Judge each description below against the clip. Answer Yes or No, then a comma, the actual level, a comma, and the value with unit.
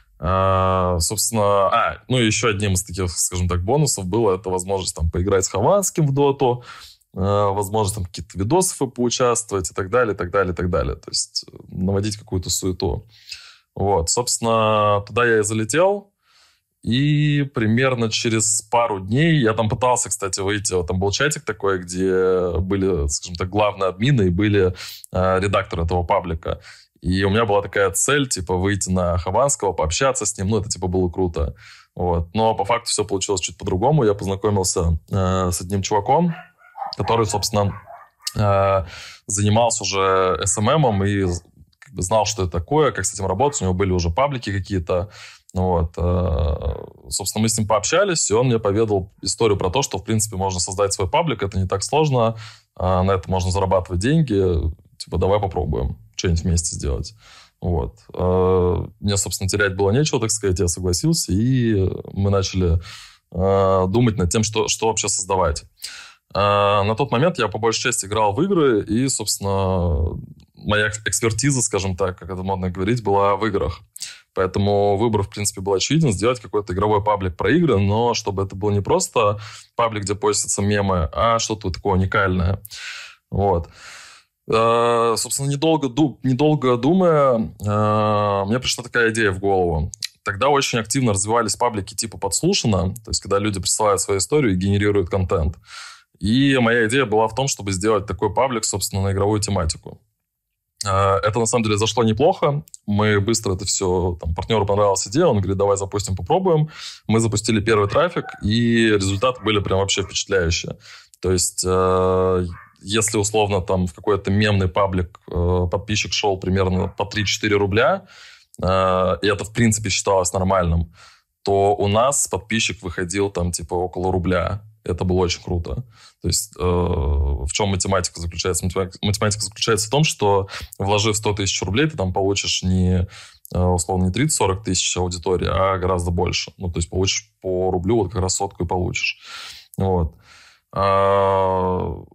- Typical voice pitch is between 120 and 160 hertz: No, low, 100 Hz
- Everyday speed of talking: No, fast, 165 wpm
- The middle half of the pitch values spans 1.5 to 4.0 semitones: Yes, average, 3.1 semitones